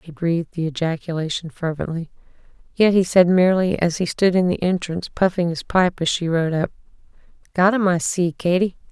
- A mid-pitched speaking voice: Yes, medium, 175 Hz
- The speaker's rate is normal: Yes, average, 180 wpm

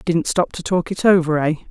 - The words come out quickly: Yes, fast, 210 wpm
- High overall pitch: No, medium, 170 Hz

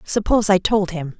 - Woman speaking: Yes, female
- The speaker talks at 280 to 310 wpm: No, average, 200 wpm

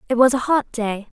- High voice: Yes, high, 240 Hz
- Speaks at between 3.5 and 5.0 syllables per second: No, 5.5 syllables/s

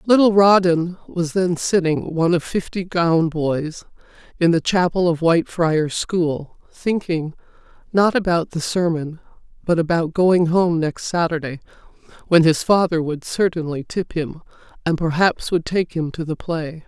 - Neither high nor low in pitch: Yes, medium, 170 Hz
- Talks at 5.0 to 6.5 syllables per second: No, 4.3 syllables/s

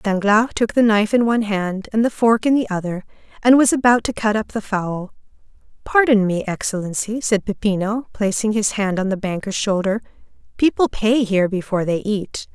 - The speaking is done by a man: No, female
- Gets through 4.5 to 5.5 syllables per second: Yes, 5.3 syllables/s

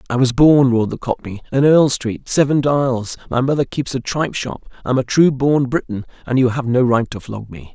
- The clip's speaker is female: No, male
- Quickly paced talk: Yes, fast, 225 wpm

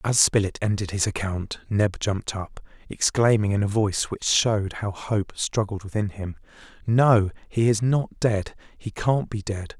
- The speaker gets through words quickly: No, average, 170 wpm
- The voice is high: No, low, 105 Hz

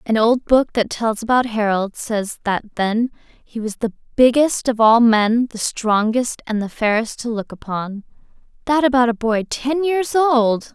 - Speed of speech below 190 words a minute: Yes, average, 180 wpm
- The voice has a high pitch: Yes, high, 235 Hz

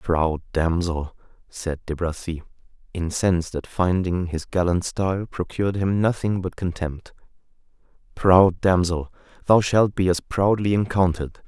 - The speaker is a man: Yes, male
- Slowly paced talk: Yes, slow, 120 wpm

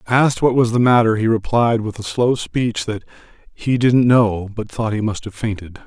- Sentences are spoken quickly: Yes, fast, 215 wpm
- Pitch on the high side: No, low, 115 Hz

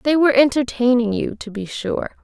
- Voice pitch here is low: No, very high, 250 Hz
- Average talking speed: Yes, average, 190 wpm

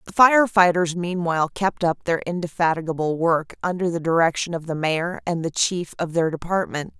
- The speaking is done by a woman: Yes, female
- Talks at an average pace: Yes, average, 180 wpm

